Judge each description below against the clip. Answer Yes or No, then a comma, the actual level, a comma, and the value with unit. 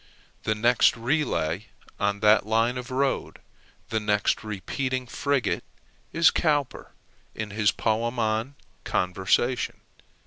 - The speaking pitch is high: No, low, 115 Hz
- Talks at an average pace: No, slow, 110 wpm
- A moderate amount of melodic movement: Yes, average, 3.5 semitones